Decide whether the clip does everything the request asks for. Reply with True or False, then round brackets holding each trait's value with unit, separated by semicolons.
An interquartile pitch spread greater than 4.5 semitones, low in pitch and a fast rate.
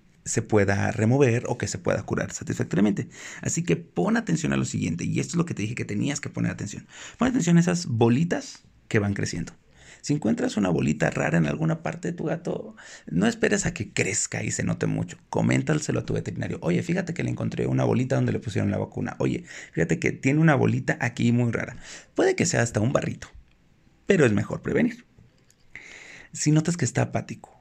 True (5.6 semitones; 120 Hz; 210 wpm)